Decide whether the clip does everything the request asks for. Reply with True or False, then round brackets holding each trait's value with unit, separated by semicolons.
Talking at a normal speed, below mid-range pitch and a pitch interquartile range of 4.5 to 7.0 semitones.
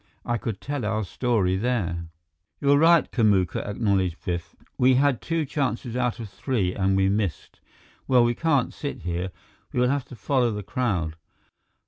True (165 wpm; 115 Hz; 5.2 semitones)